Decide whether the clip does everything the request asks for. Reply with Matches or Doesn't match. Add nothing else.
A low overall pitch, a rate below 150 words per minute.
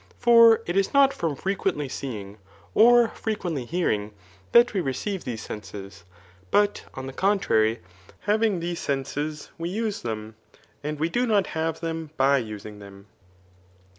Doesn't match